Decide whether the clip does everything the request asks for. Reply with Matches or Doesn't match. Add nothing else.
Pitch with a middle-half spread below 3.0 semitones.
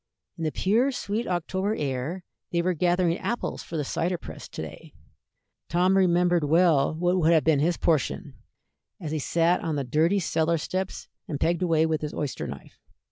Matches